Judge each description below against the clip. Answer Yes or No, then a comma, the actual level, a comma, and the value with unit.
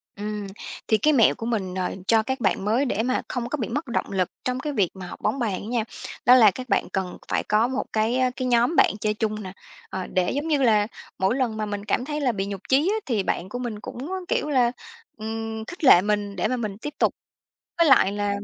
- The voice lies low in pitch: No, high, 225 Hz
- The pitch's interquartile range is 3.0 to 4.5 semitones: Yes, average, 3.8 semitones